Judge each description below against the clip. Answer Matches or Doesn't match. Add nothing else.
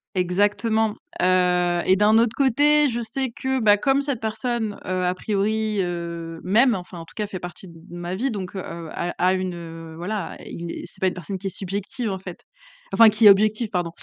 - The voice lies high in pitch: Matches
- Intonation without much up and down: Doesn't match